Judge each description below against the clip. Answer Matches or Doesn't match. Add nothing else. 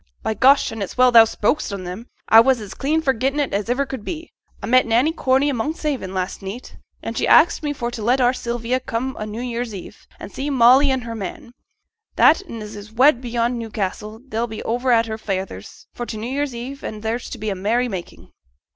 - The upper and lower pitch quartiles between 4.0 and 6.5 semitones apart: Doesn't match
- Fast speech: Matches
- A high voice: Matches